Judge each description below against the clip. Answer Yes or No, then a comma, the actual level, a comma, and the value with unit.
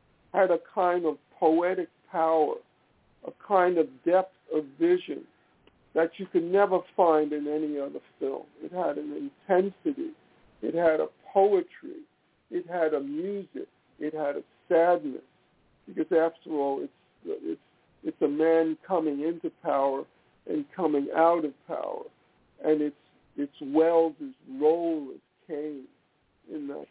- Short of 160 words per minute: Yes, average, 140 wpm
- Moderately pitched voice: Yes, medium, 165 Hz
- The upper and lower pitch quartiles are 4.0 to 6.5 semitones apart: Yes, average, 4.4 semitones